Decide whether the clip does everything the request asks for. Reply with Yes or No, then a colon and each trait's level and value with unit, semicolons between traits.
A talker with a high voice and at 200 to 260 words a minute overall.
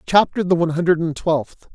No: medium, 170 Hz; fast, 205 wpm